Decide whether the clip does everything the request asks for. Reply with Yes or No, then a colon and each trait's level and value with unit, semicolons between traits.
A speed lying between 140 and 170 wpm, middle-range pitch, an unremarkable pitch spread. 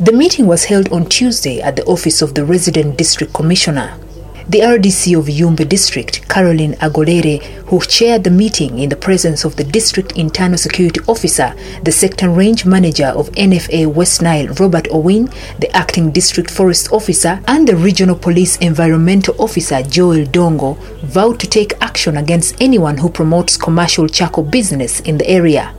Yes: average, 165 wpm; medium, 175 Hz; average, 3.2 semitones